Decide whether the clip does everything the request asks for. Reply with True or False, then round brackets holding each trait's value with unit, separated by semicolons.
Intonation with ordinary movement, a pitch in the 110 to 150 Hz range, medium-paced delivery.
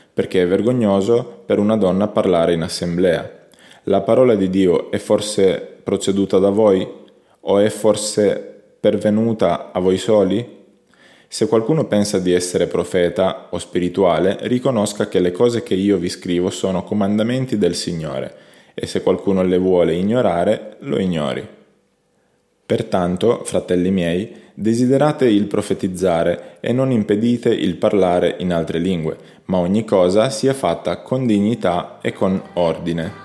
False (3.4 semitones; 100 Hz; 140 wpm)